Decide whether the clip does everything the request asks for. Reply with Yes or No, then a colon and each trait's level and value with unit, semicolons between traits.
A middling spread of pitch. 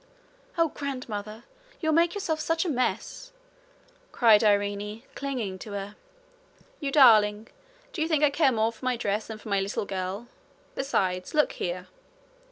No: wide, 5.8 semitones